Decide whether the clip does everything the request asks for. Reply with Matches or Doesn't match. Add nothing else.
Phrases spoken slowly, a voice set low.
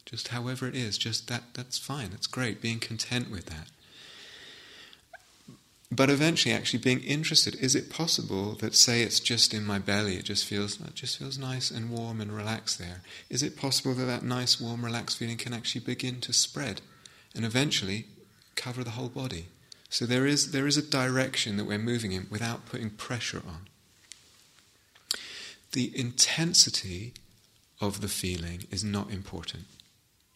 Doesn't match